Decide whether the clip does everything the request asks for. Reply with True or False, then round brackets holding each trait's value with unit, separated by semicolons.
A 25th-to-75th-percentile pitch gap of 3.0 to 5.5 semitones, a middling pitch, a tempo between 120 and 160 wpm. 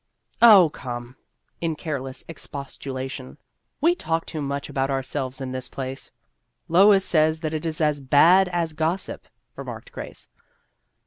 True (3.8 semitones; 150 Hz; 150 wpm)